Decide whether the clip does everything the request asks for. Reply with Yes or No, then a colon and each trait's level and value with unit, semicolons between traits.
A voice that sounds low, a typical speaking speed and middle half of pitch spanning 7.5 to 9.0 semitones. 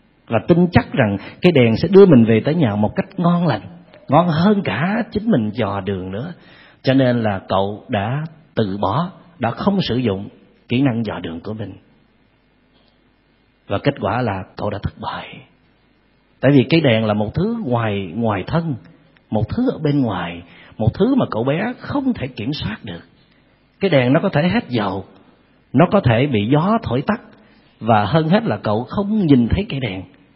Yes: low, 125 Hz; average, 195 wpm; wide, 8.4 semitones